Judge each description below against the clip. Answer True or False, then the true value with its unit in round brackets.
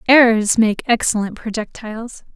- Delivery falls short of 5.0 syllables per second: True (4.8 syllables/s)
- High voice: True (225 Hz)